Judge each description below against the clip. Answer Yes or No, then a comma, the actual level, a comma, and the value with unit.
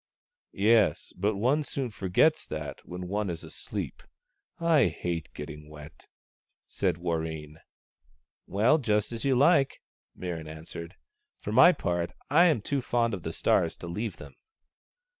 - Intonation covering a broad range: Yes, wide, 7.4 semitones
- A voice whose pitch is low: Yes, low, 100 Hz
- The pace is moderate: Yes, average, 155 wpm